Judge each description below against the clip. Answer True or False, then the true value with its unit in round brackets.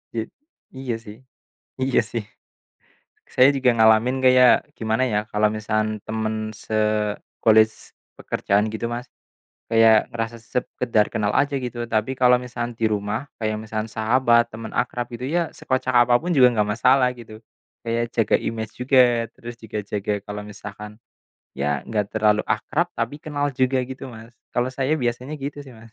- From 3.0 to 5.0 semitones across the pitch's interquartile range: False (2.6 semitones)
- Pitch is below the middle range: True (115 Hz)